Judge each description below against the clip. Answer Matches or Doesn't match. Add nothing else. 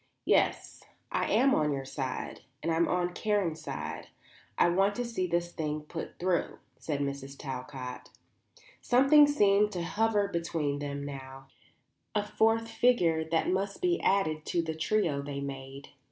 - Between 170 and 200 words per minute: Doesn't match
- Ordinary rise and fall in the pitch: Doesn't match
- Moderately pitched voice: Matches